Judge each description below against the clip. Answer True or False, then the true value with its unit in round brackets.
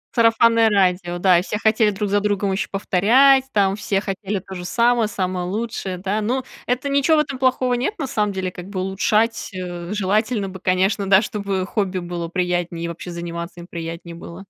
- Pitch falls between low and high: False (195 Hz)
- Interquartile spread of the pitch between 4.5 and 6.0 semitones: False (3.6 semitones)